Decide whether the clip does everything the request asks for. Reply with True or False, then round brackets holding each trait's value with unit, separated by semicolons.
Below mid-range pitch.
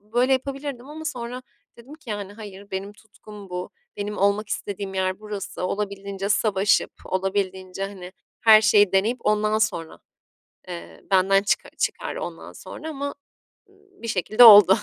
False (205 Hz)